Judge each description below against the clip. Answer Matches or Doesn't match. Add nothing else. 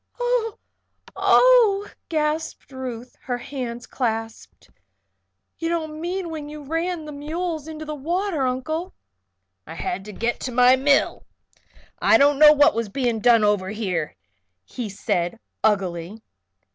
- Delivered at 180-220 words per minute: Doesn't match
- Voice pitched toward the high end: Matches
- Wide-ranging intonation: Matches